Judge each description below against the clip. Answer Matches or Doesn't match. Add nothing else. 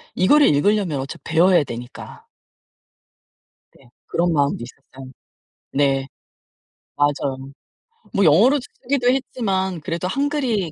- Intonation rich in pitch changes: Matches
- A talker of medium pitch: Matches